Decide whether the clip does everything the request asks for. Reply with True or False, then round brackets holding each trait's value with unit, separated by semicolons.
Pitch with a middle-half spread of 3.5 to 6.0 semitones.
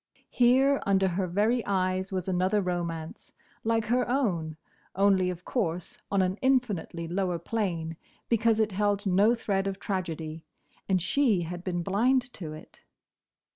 True (4.0 semitones)